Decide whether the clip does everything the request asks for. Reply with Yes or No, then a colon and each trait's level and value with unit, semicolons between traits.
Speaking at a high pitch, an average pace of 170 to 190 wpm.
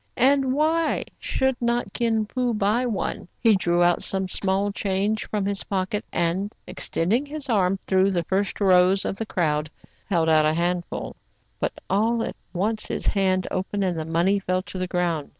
Yes: high, 195 Hz; average, 185 wpm